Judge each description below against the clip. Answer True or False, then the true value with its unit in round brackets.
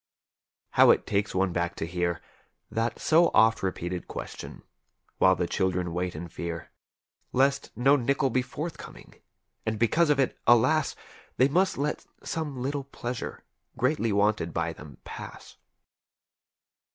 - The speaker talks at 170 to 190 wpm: False (140 wpm)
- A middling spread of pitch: False (7.4 semitones)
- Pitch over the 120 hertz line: False (115 Hz)